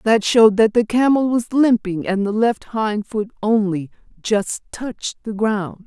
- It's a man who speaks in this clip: No, female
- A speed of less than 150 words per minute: No, average, 175 wpm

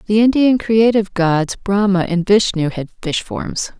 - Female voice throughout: Yes, female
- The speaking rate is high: No, average, 160 wpm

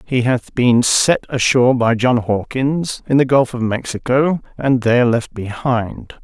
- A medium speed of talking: Yes, average, 165 wpm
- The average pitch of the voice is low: Yes, low, 125 Hz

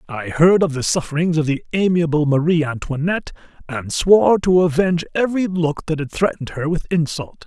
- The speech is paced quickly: No, average, 175 wpm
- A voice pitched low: No, medium, 160 Hz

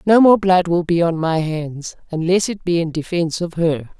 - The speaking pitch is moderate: Yes, medium, 170 Hz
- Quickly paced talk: Yes, fast, 225 wpm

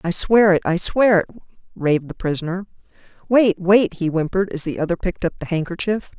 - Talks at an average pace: Yes, average, 195 wpm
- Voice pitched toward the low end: No, medium, 185 Hz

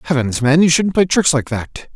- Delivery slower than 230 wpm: No, fast, 245 wpm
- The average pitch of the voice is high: No, medium, 150 Hz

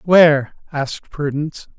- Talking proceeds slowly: Yes, slow, 100 wpm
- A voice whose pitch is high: No, medium, 150 Hz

